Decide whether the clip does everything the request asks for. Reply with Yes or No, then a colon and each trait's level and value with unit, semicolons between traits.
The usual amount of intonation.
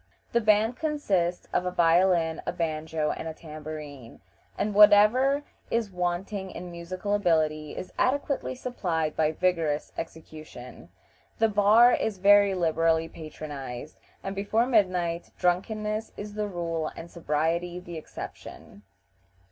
Yes: average, 4.4 semitones